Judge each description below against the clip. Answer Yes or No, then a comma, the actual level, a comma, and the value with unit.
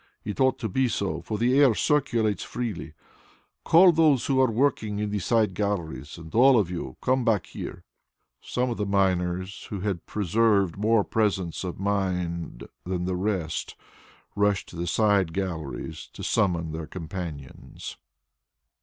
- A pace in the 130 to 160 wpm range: Yes, average, 155 wpm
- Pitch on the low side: Yes, low, 100 Hz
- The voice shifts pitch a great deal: No, average, 4.4 semitones